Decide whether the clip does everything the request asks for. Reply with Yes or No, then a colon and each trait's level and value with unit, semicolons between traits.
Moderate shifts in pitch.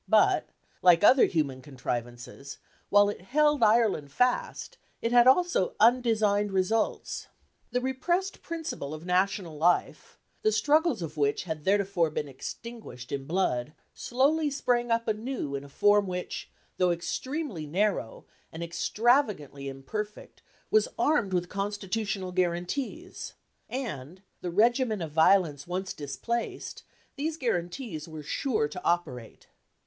No: wide, 7.2 semitones